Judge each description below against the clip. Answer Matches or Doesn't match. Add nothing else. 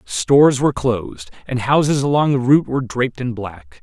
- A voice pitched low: Matches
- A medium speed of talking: Matches